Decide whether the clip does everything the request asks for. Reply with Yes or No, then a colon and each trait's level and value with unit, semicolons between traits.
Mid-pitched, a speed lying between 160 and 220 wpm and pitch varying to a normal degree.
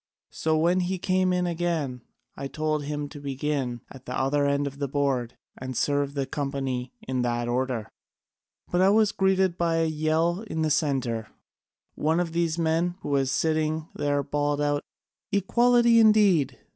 Yes: medium, 150 Hz; average, 170 wpm; average, 3.9 semitones